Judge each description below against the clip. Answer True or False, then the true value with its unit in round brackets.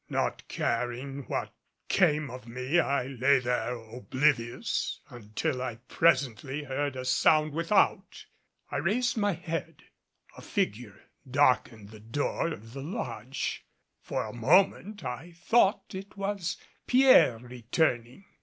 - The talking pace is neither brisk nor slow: False (125 wpm)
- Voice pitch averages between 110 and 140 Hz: True (135 Hz)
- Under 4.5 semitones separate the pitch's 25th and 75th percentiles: False (5.4 semitones)